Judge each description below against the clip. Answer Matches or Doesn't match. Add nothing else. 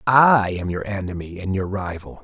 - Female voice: Doesn't match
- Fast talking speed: Doesn't match